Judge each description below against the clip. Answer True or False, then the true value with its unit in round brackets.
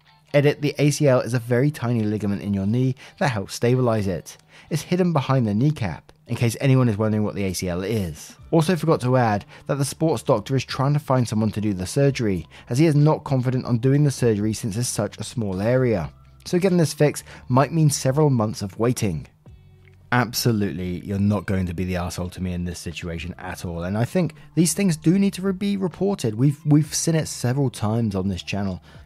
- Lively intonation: True (6.3 semitones)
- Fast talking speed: True (215 wpm)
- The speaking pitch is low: True (120 Hz)